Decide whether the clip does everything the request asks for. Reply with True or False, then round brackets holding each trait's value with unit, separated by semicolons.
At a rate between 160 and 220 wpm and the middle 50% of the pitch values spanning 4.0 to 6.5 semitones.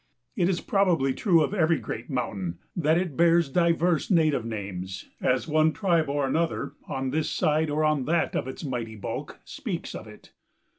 True (180 wpm; 4.3 semitones)